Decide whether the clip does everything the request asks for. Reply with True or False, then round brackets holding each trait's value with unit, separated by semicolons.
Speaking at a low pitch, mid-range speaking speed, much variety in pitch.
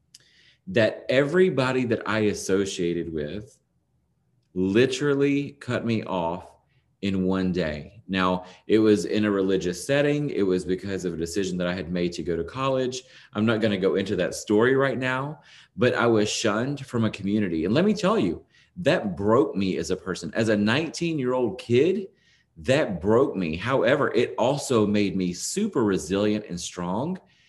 True (110 Hz; 175 wpm; 6.2 semitones)